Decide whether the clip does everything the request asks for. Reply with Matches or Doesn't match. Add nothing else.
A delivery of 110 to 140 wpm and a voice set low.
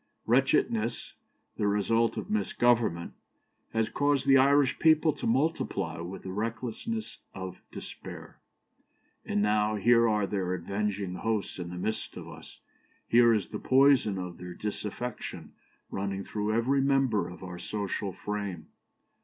Matches